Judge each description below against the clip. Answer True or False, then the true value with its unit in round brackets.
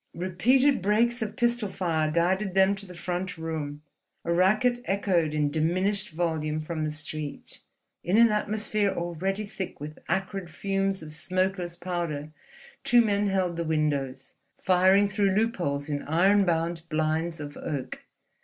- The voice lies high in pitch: False (180 Hz)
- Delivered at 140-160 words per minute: True (145 wpm)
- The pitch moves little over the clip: False (4.0 semitones)